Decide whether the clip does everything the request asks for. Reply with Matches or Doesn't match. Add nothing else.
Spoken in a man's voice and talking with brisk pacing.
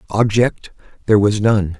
Doesn't match